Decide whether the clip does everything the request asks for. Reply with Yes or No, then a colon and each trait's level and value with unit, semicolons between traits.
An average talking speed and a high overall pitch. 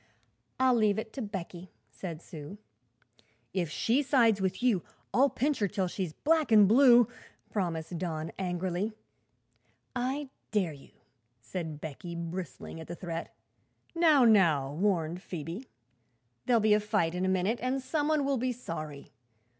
Yes: average, 150 wpm; high, 195 Hz